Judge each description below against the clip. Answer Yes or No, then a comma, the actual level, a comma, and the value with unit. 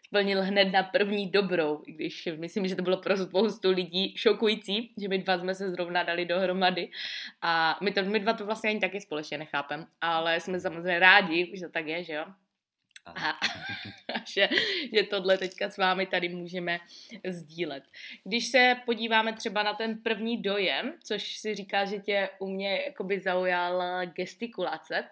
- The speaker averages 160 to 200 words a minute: Yes, fast, 170 wpm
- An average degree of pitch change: Yes, average, 3.0 semitones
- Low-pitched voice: No, high, 190 Hz